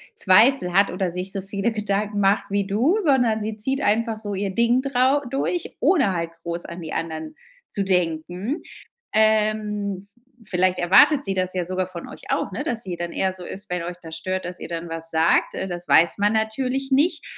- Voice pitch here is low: No, high, 200 Hz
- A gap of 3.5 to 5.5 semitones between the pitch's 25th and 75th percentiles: Yes, average, 3.9 semitones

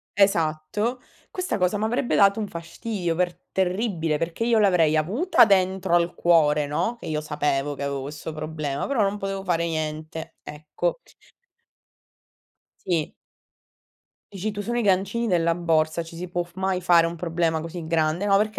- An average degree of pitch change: Yes, average, 4.0 semitones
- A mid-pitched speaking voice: Yes, medium, 175 Hz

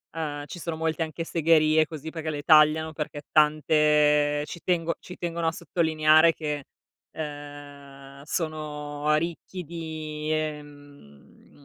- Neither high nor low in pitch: Yes, medium, 155 Hz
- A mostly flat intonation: Yes, narrow, 1.6 semitones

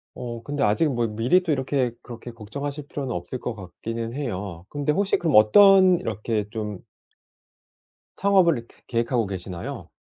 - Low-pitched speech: Yes, low, 120 Hz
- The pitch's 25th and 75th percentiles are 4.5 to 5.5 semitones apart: Yes, average, 5.2 semitones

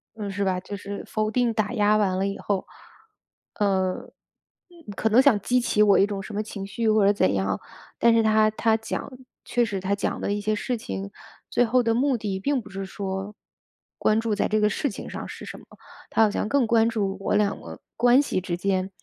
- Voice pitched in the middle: No, high, 210 Hz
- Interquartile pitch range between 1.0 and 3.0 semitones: Yes, narrow, 2.4 semitones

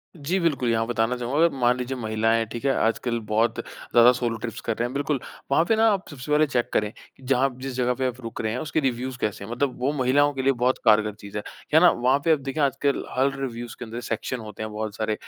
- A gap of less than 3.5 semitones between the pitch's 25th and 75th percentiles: Yes, average, 3.1 semitones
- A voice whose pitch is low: Yes, low, 125 Hz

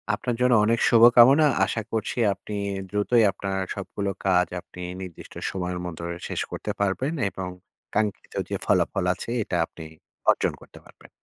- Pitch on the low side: Yes, low, 100 Hz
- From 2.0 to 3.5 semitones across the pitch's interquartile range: No, average, 4.0 semitones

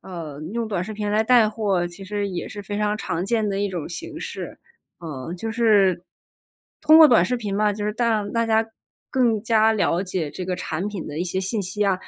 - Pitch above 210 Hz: No, high, 205 Hz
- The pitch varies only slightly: No, average, 3.3 semitones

